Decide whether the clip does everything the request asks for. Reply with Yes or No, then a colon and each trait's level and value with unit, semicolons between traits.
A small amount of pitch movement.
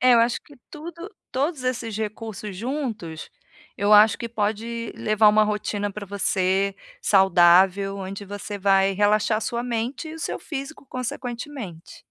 No: average, 3.8 semitones